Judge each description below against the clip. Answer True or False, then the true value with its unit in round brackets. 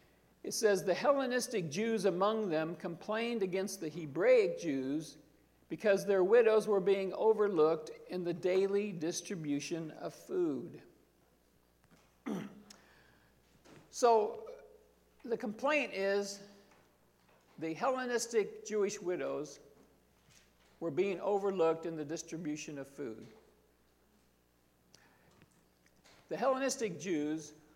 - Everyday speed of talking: False (95 wpm)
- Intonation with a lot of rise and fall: True (6.3 semitones)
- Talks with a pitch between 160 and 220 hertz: True (185 Hz)